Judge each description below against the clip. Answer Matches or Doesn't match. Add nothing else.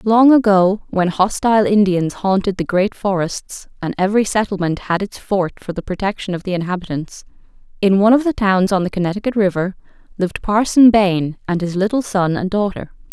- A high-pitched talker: Matches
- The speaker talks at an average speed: Matches